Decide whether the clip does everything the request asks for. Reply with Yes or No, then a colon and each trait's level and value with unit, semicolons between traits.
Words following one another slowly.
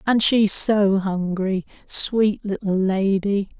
Yes: slow, 115 wpm